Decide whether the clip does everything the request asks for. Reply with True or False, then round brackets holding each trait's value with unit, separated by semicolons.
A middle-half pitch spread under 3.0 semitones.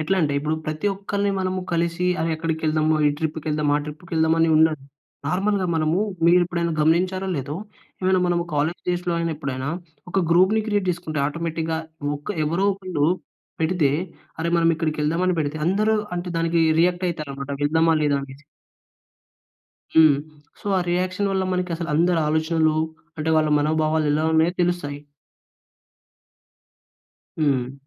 True (2.6 semitones)